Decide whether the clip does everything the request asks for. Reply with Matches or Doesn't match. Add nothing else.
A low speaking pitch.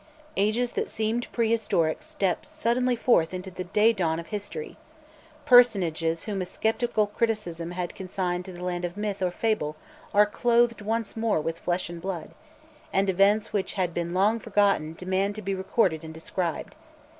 Doesn't match